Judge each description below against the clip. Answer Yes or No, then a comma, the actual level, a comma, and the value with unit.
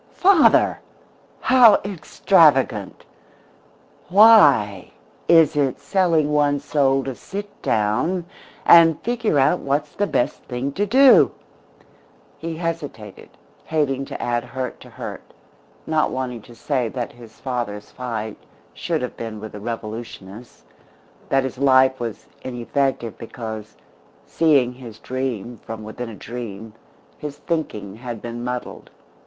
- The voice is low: Yes, low, 130 Hz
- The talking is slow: Yes, slow, 125 wpm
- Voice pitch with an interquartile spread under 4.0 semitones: No, average, 5.2 semitones